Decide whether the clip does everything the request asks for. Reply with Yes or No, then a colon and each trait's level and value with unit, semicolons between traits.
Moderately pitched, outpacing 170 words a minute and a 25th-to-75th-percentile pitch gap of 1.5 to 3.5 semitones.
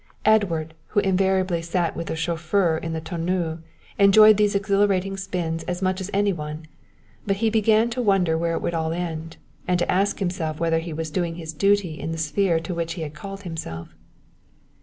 Yes: medium, 175 Hz; average, 195 wpm; average, 3.2 semitones